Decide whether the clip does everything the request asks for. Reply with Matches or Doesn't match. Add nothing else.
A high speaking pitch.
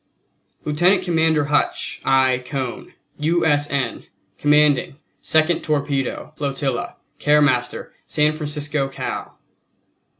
Doesn't match